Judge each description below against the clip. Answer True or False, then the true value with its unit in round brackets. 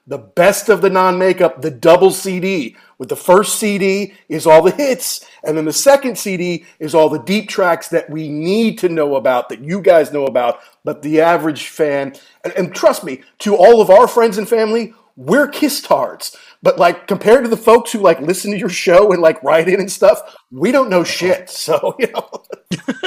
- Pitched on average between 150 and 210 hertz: True (185 Hz)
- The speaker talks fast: True (210 wpm)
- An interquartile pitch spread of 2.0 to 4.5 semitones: False (5.4 semitones)